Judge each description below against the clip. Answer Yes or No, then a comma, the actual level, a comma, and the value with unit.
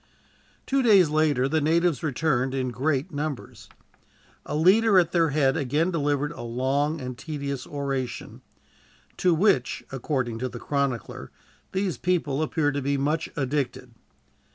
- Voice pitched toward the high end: No, medium, 145 Hz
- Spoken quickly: No, average, 140 wpm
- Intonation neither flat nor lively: Yes, average, 3.3 semitones